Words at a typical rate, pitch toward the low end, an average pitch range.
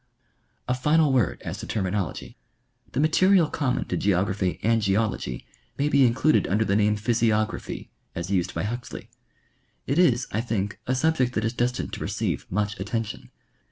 Yes: average, 170 wpm; low, 115 Hz; average, 4.0 semitones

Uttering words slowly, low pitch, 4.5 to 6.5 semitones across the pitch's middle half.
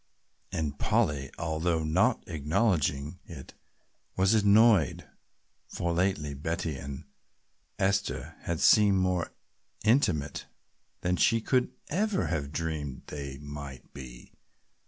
Yes: slow, 105 wpm; very low, 80 Hz; average, 5.2 semitones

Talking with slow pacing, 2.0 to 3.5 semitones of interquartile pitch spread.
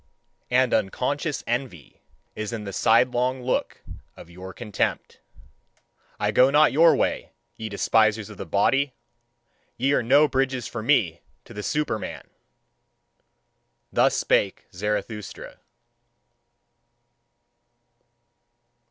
No: slow, 105 wpm; average, 4.2 semitones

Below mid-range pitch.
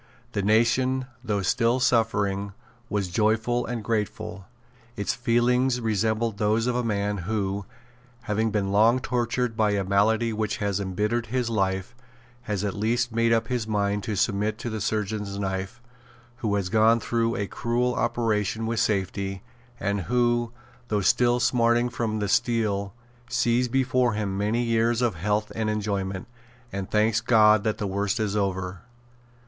Yes: low, 110 Hz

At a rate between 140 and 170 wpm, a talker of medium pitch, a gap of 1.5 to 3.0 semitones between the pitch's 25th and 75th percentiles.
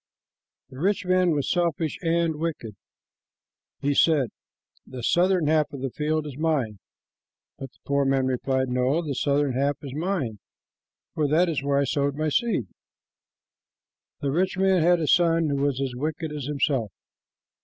No: average, 165 wpm; medium, 145 Hz; average, 3.5 semitones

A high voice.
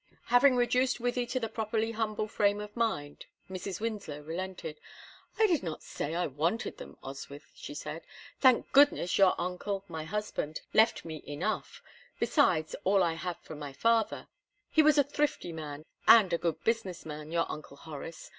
Yes: high, 195 Hz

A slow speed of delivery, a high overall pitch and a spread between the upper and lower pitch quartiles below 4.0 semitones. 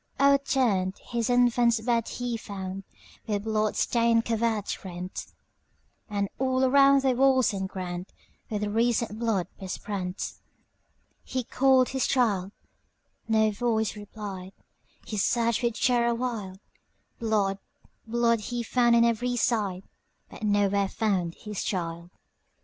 Yes: slow, 100 wpm; high, 220 Hz; average, 3.4 semitones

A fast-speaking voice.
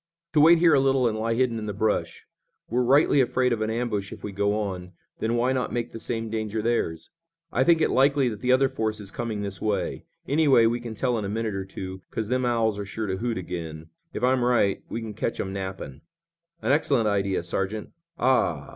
Yes: fast, 225 wpm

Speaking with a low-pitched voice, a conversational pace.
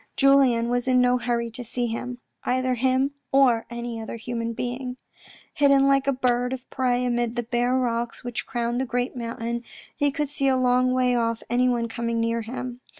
No: high, 245 Hz; average, 190 wpm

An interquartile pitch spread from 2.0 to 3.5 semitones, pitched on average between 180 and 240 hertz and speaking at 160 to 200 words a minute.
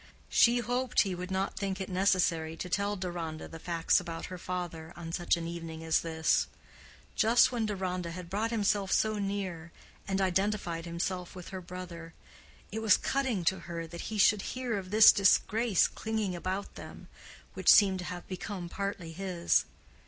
Yes: average, 3.1 semitones; medium, 185 Hz; average, 175 wpm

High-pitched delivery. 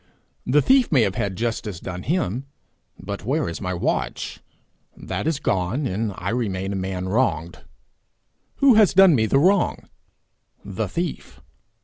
No: low, 110 Hz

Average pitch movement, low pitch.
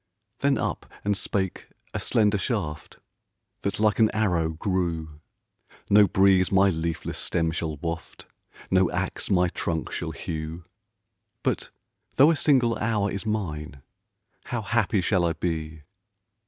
Yes: average, 4.3 semitones; very low, 95 Hz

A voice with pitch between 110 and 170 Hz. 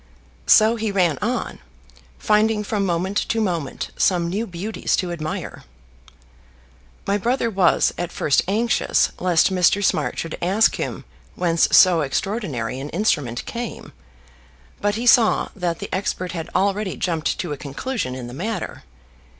No: medium, 185 Hz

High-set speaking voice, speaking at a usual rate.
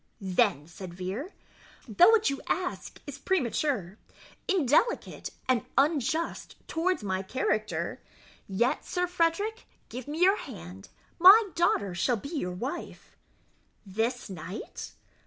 No: very high, 265 Hz; slow, 120 wpm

